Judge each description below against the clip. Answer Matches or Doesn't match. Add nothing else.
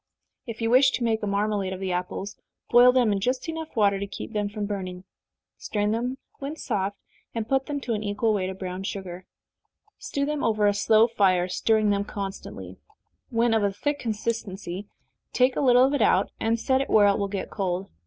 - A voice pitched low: Doesn't match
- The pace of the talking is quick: Matches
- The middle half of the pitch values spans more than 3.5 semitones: Doesn't match